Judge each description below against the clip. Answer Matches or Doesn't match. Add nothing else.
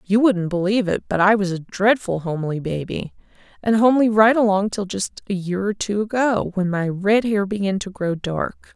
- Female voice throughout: Matches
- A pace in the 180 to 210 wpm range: Matches